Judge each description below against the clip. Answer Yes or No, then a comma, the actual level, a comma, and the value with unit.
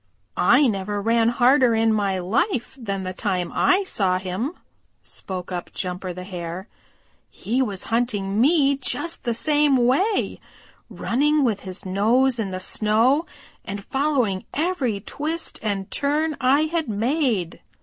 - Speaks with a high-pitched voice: Yes, high, 230 Hz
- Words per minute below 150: Yes, average, 140 wpm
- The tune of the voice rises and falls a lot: Yes, wide, 6.3 semitones